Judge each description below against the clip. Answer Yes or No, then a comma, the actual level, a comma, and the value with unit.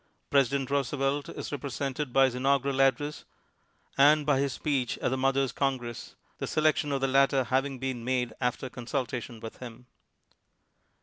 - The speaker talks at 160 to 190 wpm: Yes, average, 165 wpm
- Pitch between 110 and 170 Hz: Yes, low, 135 Hz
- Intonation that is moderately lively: No, narrow, 1.7 semitones